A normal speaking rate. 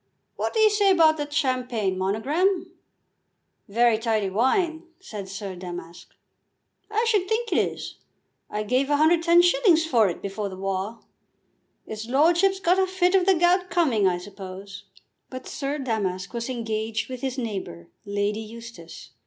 Yes: average, 150 wpm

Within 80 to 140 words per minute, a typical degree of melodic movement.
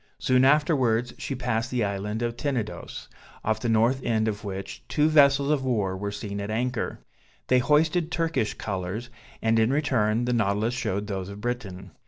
No: average, 175 wpm; average, 4.0 semitones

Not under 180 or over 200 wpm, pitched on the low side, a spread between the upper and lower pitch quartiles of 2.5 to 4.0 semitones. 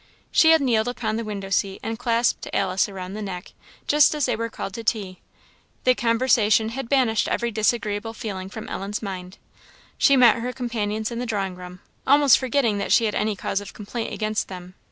No: average, 195 wpm; high, 220 Hz; average, 3.2 semitones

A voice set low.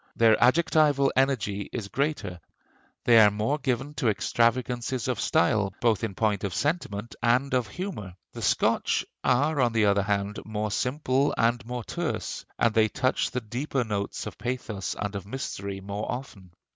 Yes: low, 115 Hz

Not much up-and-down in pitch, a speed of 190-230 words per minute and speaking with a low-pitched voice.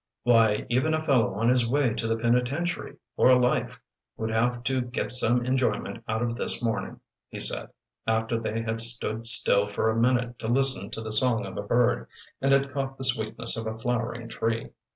Yes: narrow, 2.0 semitones; average, 195 wpm; low, 120 Hz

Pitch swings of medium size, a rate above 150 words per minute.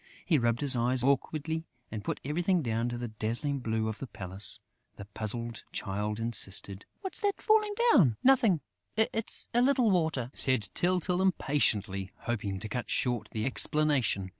No: wide, 7.3 semitones; average, 160 wpm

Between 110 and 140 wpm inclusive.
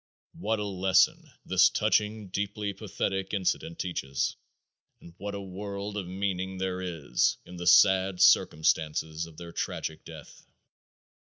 Yes: slow, 135 wpm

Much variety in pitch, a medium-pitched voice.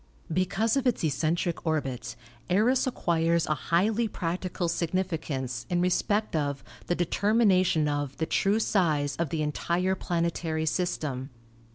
No: average, 3.5 semitones; medium, 170 Hz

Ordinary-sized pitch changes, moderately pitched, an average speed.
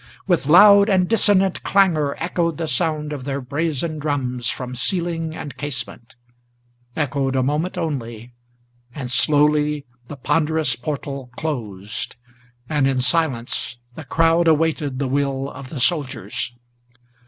No: average, 3.9 semitones; medium, 145 Hz; slow, 130 wpm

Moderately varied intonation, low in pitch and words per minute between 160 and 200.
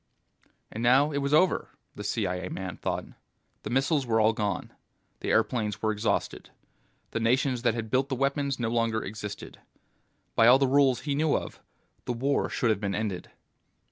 Yes: average, 4.0 semitones; low, 120 Hz; average, 175 wpm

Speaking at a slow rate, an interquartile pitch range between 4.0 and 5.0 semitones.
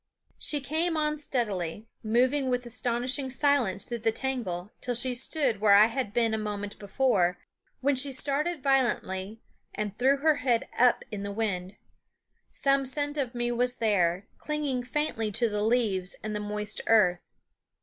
No: average, 160 wpm; average, 4.4 semitones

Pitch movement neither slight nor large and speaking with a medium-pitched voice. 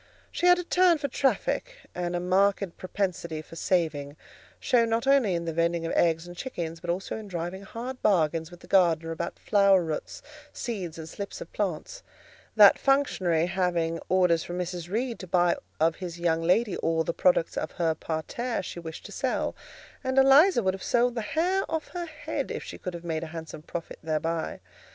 No: wide, 5.7 semitones; medium, 180 Hz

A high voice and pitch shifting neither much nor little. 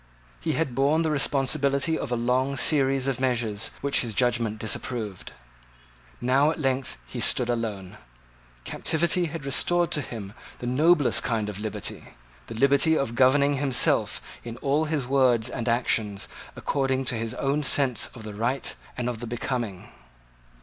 No: low, 130 Hz; average, 3.2 semitones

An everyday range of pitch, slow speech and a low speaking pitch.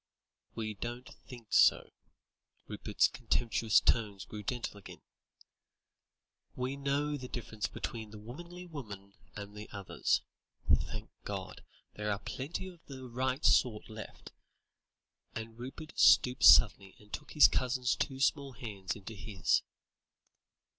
Yes: average, 4.0 semitones; slow, 125 wpm; low, 120 Hz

